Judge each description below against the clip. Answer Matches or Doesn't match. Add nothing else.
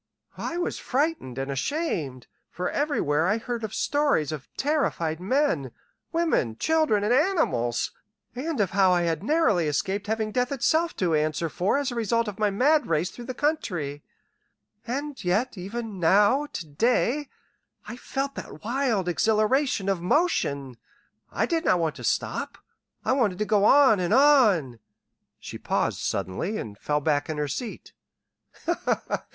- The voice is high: Matches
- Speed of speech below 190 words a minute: Matches